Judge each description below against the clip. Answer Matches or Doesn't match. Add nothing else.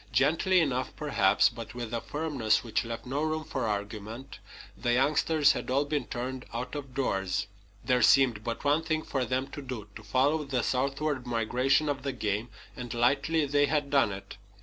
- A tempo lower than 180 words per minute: Doesn't match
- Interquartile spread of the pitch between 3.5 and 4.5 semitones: Matches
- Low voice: Matches